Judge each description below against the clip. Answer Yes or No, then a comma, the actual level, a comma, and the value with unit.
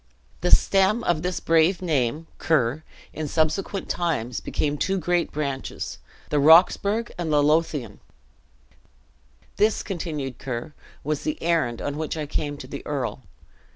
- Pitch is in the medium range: Yes, medium, 155 Hz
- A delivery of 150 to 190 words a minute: No, slow, 135 wpm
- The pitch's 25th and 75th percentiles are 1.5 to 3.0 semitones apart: No, average, 3.7 semitones